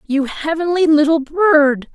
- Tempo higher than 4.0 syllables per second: No, 3.9 syllables/s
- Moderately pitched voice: No, very high, 305 Hz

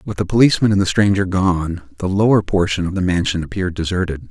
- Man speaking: Yes, male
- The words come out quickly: Yes, fast, 210 wpm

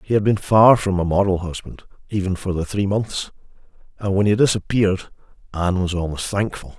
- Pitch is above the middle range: No, very low, 95 Hz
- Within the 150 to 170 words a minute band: No, average, 185 wpm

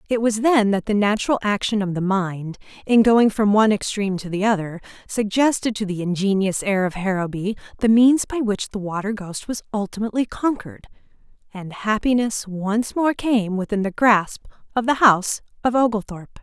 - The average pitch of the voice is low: No, high, 210 Hz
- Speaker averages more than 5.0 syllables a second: Yes, 5.4 syllables/s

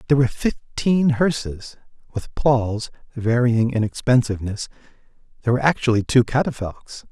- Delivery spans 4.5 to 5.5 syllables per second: Yes, 5.4 syllables/s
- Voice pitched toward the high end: No, low, 120 Hz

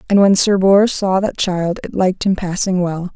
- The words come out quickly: Yes, fast, 230 wpm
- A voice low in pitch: No, high, 190 Hz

